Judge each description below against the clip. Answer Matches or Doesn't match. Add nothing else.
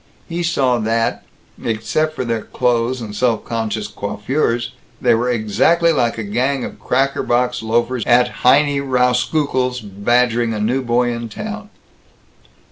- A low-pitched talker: Matches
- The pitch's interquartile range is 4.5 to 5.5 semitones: Doesn't match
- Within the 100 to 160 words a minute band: Matches